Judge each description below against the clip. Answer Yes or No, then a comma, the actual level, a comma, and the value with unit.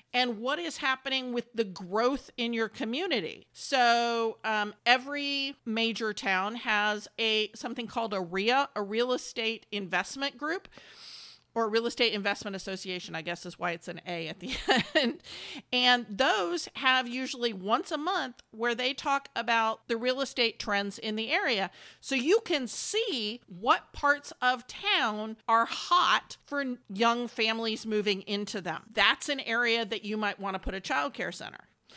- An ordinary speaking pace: Yes, average, 165 wpm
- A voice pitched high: Yes, high, 235 Hz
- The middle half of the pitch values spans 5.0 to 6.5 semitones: No, average, 3.9 semitones